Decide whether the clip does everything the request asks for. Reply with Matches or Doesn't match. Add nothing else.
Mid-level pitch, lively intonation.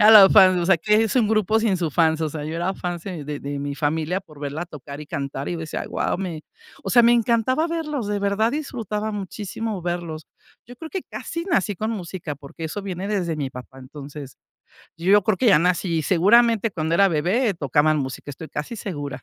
Matches